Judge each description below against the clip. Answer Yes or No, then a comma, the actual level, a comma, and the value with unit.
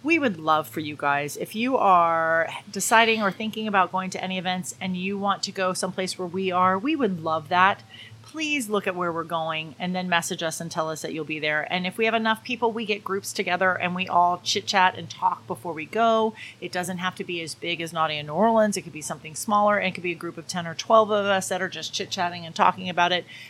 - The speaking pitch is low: No, medium, 185 Hz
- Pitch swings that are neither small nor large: Yes, average, 3.3 semitones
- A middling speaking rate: No, fast, 270 wpm